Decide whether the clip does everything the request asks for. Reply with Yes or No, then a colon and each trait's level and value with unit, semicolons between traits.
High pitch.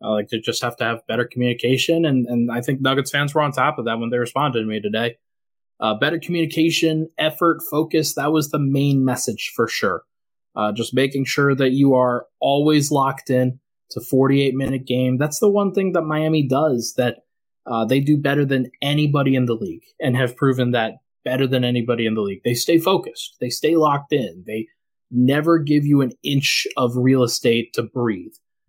No: low, 135 Hz